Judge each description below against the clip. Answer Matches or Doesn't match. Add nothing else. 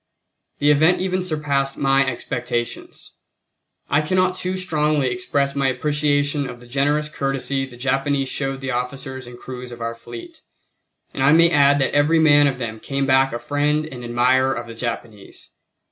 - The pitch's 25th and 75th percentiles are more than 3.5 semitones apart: Doesn't match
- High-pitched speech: Doesn't match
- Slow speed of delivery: Doesn't match